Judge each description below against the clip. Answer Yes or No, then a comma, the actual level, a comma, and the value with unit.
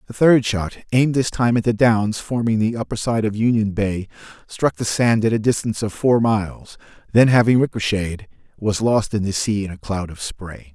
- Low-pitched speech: Yes, low, 110 Hz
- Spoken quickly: Yes, fast, 210 wpm